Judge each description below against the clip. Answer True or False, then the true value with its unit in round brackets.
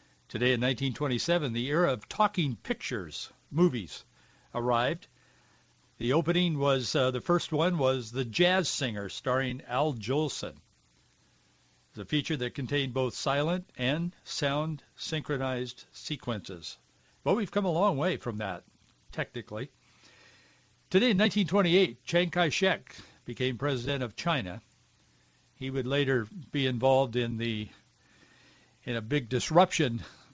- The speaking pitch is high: False (135 Hz)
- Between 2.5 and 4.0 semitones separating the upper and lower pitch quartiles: False (5.3 semitones)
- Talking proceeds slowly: True (130 wpm)